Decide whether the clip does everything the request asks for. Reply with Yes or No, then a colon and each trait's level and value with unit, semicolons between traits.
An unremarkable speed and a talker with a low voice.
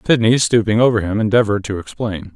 Yes: average, 180 wpm; low, 110 Hz